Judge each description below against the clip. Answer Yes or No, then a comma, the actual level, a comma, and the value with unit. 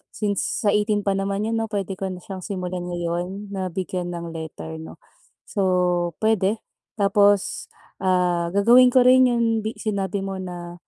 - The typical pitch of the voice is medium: No, high, 195 Hz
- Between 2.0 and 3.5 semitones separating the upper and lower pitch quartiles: Yes, narrow, 2.6 semitones